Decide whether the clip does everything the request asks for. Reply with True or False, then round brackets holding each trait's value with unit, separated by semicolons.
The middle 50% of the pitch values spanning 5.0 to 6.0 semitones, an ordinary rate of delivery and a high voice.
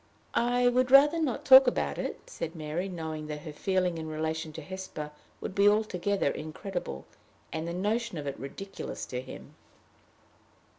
False (5.6 semitones; 165 wpm; 180 Hz)